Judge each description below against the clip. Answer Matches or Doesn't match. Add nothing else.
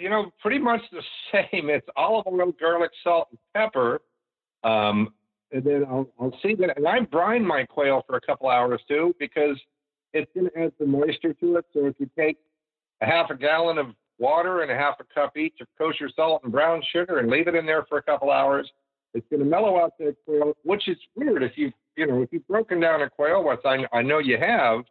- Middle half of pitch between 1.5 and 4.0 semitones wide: Matches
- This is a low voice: Doesn't match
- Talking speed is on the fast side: Matches